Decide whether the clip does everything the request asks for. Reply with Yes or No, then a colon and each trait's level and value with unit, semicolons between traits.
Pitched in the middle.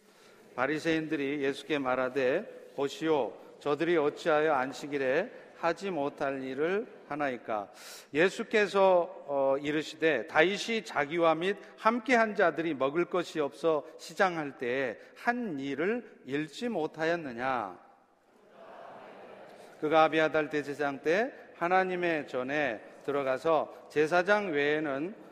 Yes: medium, 155 Hz